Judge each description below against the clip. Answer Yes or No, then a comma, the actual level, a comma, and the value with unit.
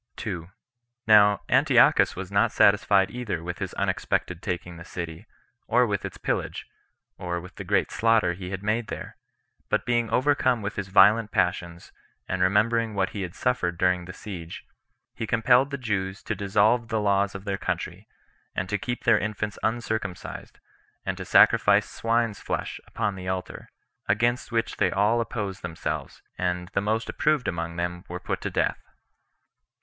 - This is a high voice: No, low, 100 Hz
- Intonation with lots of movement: No, average, 3.7 semitones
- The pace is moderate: Yes, average, 165 wpm